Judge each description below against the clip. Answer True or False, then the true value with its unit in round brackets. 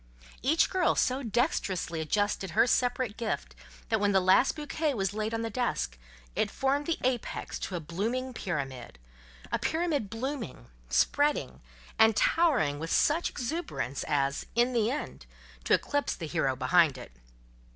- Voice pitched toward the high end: True (220 Hz)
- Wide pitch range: True (8.8 semitones)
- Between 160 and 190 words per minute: False (150 wpm)